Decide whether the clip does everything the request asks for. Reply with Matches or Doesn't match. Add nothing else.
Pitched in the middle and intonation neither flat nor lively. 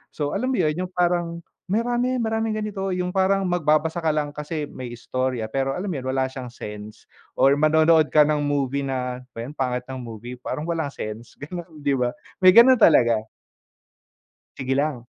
Doesn't match